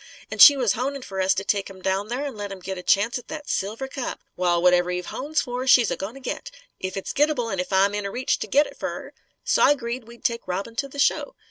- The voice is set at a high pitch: Yes, high, 225 Hz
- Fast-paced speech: Yes, fast, 275 wpm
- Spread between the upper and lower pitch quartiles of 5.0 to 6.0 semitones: Yes, wide, 5.5 semitones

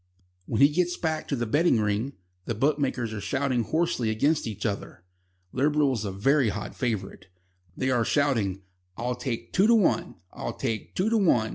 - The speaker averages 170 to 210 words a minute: Yes, average, 180 wpm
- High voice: No, low, 125 Hz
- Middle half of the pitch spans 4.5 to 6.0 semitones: Yes, average, 5.3 semitones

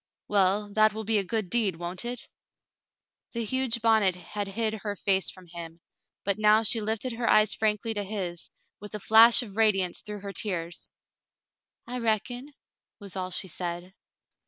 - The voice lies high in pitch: Yes, high, 210 Hz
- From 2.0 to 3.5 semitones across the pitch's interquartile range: Yes, average, 2.8 semitones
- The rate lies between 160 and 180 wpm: Yes, average, 175 wpm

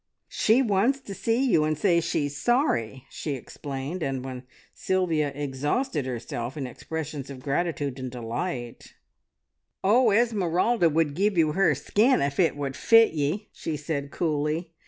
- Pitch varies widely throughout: Yes, wide, 5.8 semitones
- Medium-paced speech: Yes, average, 150 wpm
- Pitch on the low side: No, medium, 155 Hz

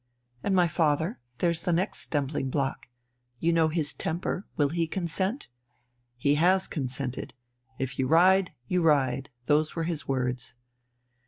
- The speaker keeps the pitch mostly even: No, average, 4.1 semitones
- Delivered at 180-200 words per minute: No, average, 145 wpm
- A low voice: No, medium, 160 Hz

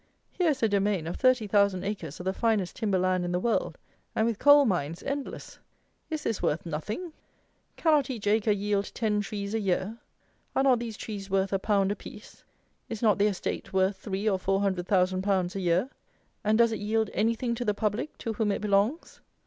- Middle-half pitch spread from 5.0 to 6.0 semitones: No, average, 2.9 semitones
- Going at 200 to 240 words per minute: Yes, fast, 205 wpm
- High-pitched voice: Yes, high, 205 Hz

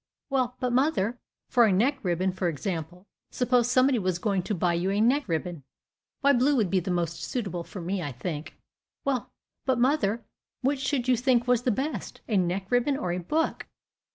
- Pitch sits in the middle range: No, high, 220 Hz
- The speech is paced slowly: No, average, 195 wpm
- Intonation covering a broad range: Yes, wide, 6.0 semitones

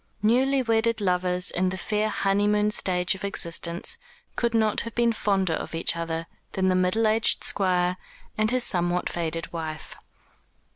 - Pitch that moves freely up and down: No, average, 3.5 semitones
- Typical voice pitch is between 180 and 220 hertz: Yes, high, 190 Hz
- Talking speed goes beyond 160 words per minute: No, average, 155 wpm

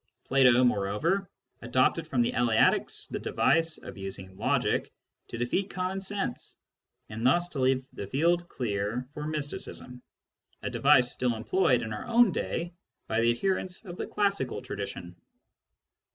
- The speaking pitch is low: Yes, low, 130 Hz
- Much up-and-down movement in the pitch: Yes, wide, 6.9 semitones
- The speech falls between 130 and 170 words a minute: Yes, average, 150 wpm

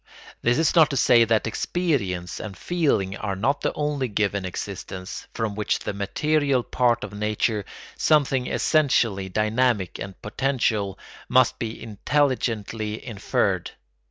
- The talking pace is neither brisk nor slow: No, slow, 130 wpm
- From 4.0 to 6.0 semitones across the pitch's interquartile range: Yes, average, 4.9 semitones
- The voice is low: Yes, low, 115 Hz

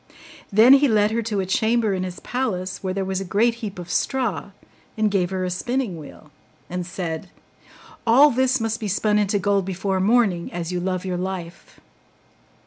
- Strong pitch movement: No, average, 3.6 semitones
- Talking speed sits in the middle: Yes, average, 190 wpm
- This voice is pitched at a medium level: No, high, 195 Hz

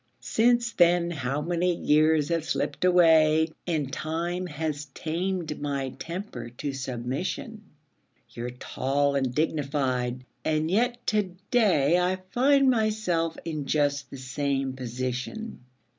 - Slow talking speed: Yes, slow, 120 wpm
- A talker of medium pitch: Yes, medium, 155 Hz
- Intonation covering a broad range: No, average, 4.7 semitones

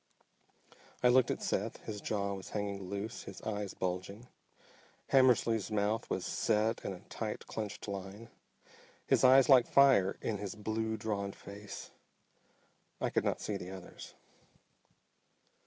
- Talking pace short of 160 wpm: Yes, average, 140 wpm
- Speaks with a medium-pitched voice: No, low, 105 Hz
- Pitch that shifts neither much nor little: No, narrow, 2.2 semitones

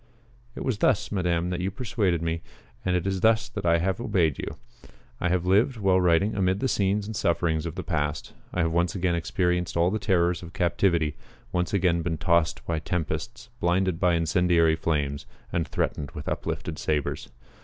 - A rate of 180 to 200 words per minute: Yes, average, 185 wpm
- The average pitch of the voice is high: No, very low, 90 Hz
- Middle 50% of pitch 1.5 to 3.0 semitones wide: Yes, narrow, 2.5 semitones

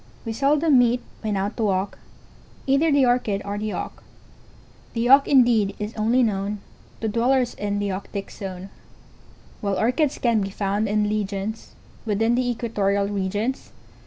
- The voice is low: No, high, 215 Hz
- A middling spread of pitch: Yes, average, 3.4 semitones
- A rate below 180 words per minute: Yes, average, 160 wpm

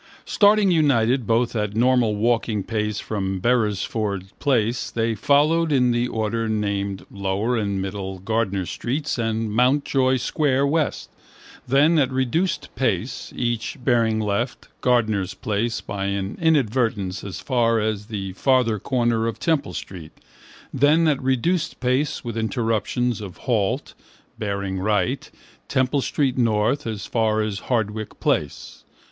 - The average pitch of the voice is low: Yes, low, 115 Hz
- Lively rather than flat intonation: No, average, 3.8 semitones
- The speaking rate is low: Yes, slow, 130 wpm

